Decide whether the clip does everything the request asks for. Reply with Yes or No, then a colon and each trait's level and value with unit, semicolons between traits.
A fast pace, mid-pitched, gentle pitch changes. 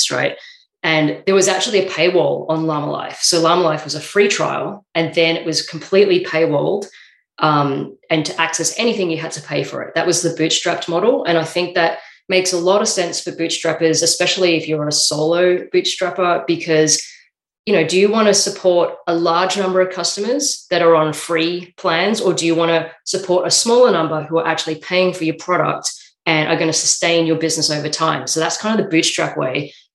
Yes: fast, 210 wpm; medium, 170 Hz; narrow, 2.2 semitones